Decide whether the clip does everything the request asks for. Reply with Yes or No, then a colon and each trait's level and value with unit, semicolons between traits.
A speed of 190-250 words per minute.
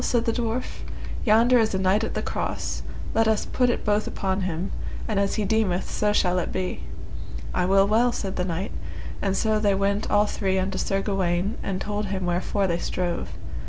Yes: average, 200 wpm